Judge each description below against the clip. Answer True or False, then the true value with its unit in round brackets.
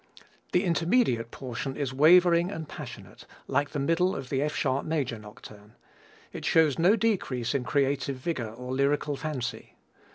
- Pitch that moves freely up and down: False (4.7 semitones)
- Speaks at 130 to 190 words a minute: True (155 wpm)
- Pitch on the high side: False (140 Hz)